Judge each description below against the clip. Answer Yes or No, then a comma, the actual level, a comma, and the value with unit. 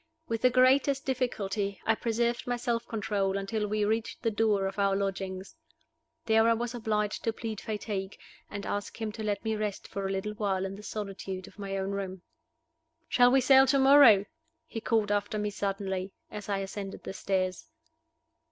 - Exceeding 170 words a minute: Yes, average, 185 wpm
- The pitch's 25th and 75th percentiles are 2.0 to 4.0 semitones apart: Yes, narrow, 2.6 semitones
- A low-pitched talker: No, high, 210 Hz